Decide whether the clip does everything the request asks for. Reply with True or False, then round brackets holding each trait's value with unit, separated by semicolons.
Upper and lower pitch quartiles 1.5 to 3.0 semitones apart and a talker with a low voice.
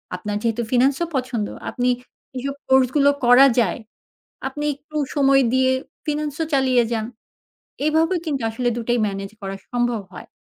False (2.7 semitones; 255 Hz)